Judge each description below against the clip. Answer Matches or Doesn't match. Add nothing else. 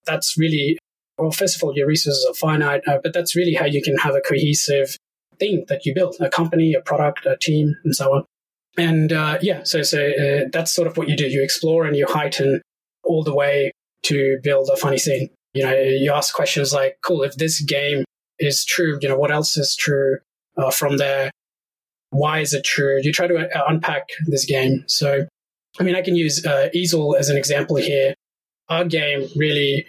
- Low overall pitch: Doesn't match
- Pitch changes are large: Doesn't match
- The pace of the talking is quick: Matches